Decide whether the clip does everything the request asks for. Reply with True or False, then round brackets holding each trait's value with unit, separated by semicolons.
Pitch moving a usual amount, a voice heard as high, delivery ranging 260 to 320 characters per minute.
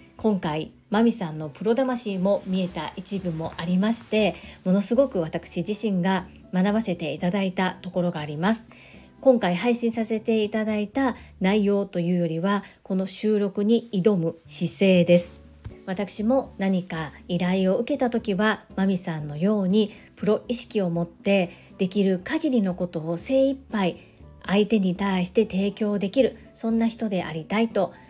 True (3.5 semitones; 195 Hz; 300 characters per minute)